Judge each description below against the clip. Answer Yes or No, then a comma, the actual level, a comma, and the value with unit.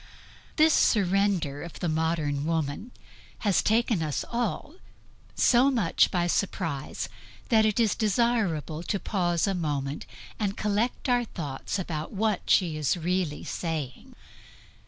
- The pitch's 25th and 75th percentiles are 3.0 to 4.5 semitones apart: No, wide, 5.5 semitones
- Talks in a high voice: No, medium, 180 Hz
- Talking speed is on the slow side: Yes, slow, 130 wpm